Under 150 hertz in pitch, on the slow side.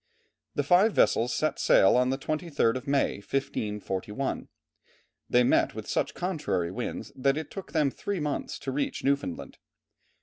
No: low, 135 Hz; average, 155 wpm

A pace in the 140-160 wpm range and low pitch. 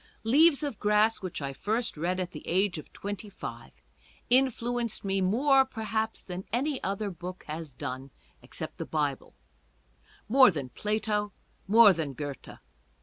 No: average, 145 wpm; high, 205 Hz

